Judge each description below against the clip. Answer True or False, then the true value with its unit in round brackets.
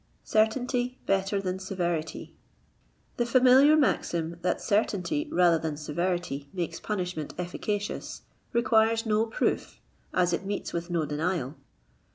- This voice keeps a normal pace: False (120 wpm)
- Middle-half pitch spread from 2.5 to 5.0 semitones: True (4.5 semitones)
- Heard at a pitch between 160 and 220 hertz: True (185 Hz)